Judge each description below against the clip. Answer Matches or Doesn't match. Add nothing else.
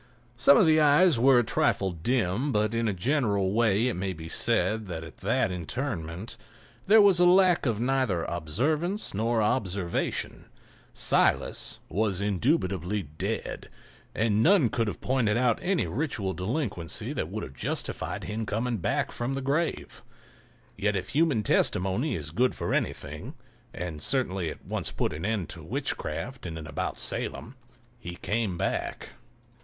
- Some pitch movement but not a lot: Doesn't match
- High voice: Doesn't match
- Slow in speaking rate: Doesn't match